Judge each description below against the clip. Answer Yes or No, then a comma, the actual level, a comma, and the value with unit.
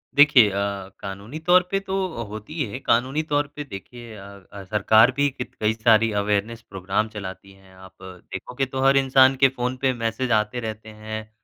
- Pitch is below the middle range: Yes, low, 115 Hz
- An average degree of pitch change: Yes, average, 4.4 semitones